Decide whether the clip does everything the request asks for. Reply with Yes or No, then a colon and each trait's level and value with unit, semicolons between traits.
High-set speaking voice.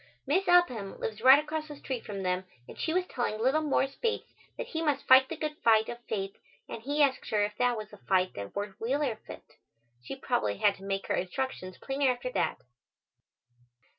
Yes: high, 245 Hz